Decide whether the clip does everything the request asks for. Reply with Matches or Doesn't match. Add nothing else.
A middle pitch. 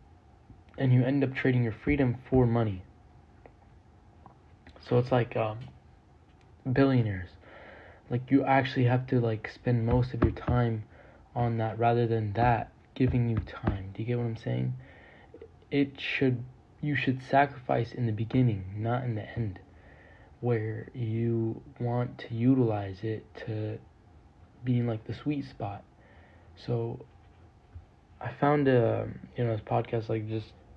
Doesn't match